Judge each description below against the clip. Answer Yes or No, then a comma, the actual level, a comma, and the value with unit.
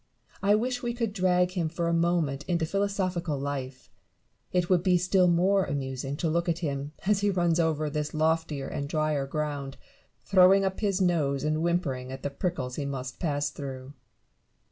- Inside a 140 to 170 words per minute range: No, average, 180 wpm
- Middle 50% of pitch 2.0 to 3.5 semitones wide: No, average, 4.3 semitones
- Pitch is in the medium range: Yes, medium, 165 Hz